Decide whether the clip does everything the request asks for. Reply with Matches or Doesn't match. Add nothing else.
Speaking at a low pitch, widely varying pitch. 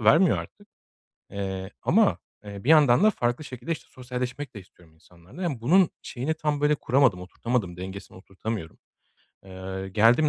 Matches